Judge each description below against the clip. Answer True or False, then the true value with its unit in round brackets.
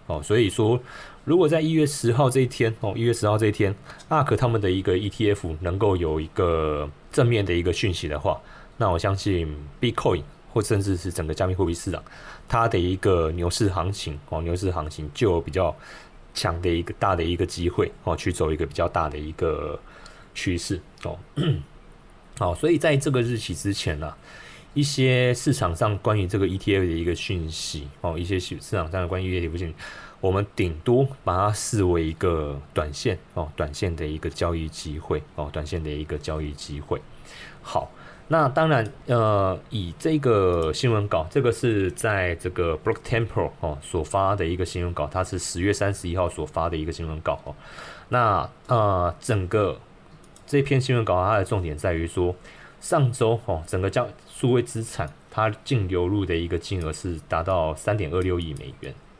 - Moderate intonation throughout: True (4.7 semitones)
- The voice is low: True (95 Hz)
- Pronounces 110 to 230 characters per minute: False (285 characters per minute)